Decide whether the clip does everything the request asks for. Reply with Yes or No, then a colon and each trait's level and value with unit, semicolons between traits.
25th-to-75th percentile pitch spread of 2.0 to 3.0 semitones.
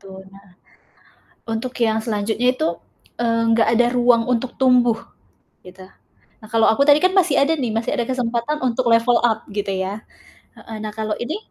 Yes: narrow, 2.5 semitones